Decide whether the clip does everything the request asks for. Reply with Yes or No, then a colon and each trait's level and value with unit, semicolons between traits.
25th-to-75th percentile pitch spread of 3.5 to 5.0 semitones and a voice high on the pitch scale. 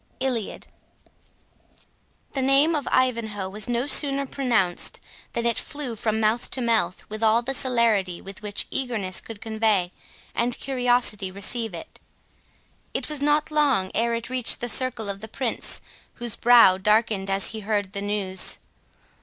Yes: average, 3.8 semitones; high, 230 Hz